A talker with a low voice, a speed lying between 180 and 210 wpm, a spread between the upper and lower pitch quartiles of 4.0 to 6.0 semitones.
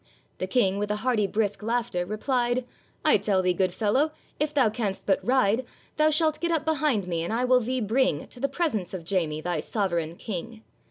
No: high, 220 Hz; fast, 205 wpm; wide, 5.4 semitones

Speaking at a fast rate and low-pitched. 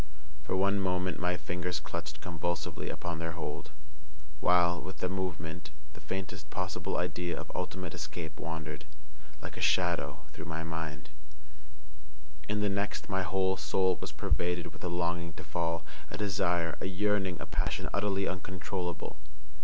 No: average, 145 wpm; very low, 85 Hz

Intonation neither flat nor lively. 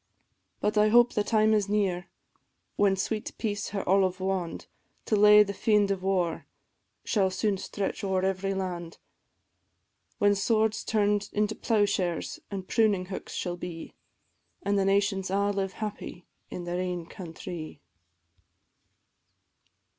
No: narrow, 2.1 semitones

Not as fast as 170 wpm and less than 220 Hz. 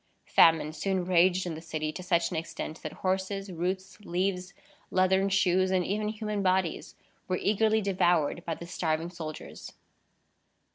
Yes: average, 150 wpm; medium, 185 Hz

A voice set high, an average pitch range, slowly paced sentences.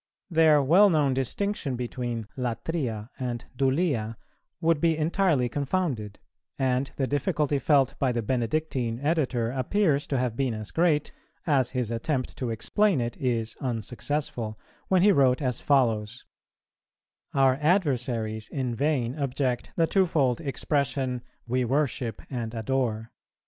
No: low, 130 Hz; average, 4.0 semitones; slow, 130 wpm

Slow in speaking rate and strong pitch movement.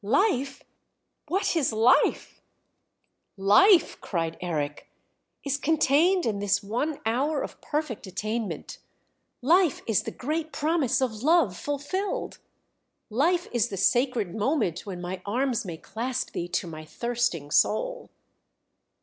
Yes: slow, 125 wpm; wide, 7.2 semitones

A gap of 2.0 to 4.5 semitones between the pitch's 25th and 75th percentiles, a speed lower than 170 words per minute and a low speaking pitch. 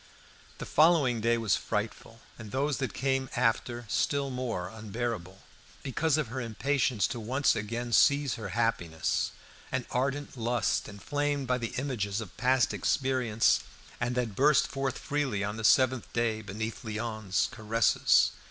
Yes: average, 3.4 semitones; average, 145 wpm; low, 120 Hz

